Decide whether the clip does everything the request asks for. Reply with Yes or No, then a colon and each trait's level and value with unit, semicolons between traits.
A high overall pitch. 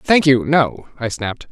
No: low, 135 Hz